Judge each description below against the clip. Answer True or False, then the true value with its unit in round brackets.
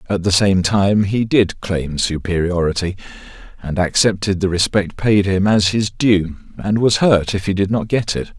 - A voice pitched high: False (95 Hz)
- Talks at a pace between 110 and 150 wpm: False (185 wpm)